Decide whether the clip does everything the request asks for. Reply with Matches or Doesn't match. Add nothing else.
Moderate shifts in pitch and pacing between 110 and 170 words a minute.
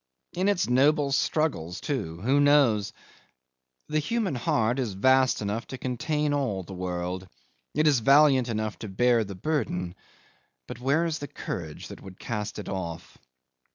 Doesn't match